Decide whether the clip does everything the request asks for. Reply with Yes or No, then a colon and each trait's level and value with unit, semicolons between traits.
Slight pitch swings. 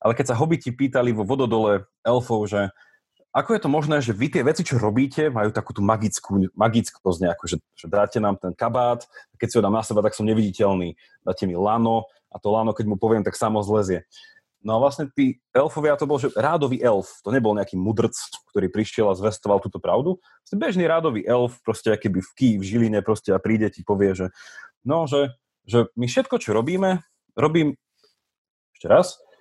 No: average, 5.1 semitones